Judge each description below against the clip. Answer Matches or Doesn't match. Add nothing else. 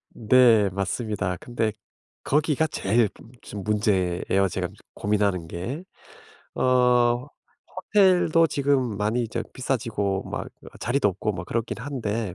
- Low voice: Matches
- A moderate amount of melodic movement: Matches